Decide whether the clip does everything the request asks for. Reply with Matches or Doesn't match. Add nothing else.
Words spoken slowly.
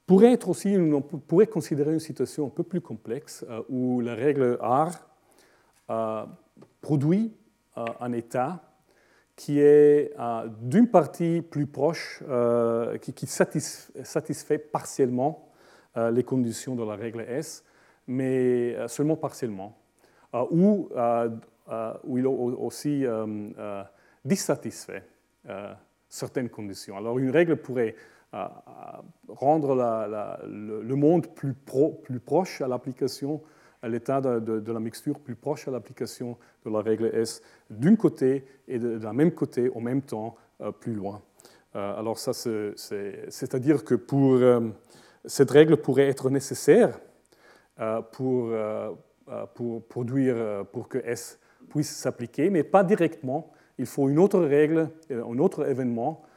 Matches